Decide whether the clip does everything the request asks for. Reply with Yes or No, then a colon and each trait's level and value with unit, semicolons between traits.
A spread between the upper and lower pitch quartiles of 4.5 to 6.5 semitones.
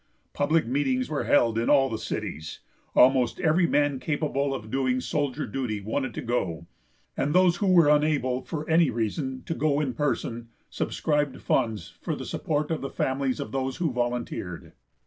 No: average, 3.4 semitones